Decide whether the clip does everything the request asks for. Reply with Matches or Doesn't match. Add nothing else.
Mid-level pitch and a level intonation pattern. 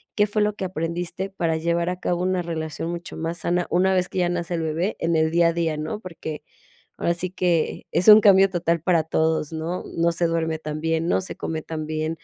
Matches